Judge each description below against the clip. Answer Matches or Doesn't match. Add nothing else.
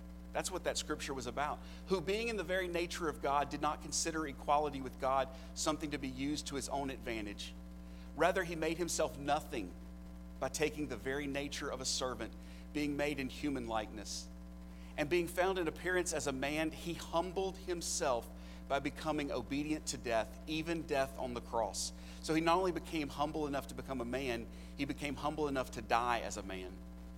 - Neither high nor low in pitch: Matches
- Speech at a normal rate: Matches